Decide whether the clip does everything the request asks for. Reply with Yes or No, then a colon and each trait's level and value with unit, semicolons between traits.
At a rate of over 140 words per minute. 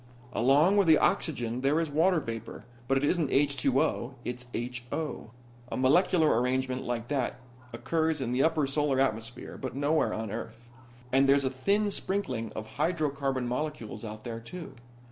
Yes: average, 160 wpm